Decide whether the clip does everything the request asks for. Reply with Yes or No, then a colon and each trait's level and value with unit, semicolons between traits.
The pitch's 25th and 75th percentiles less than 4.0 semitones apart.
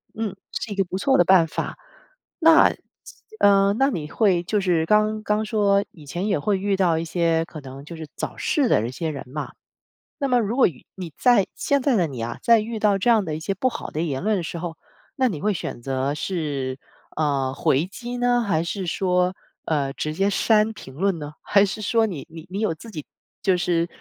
No: average, 5.2 semitones